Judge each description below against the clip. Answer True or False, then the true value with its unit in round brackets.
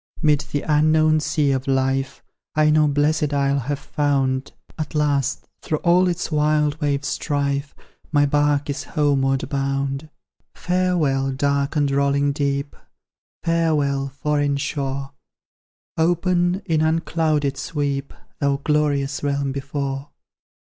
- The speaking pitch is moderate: True (145 Hz)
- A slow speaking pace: True (120 wpm)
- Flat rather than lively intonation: True (1.8 semitones)